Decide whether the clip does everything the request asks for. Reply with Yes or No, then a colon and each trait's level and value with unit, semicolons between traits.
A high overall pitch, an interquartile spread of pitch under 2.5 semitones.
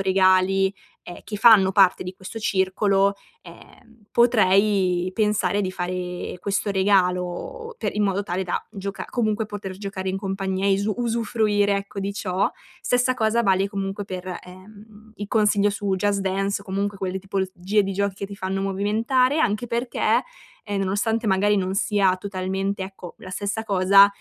Yes: high, 200 Hz; narrow, 1.7 semitones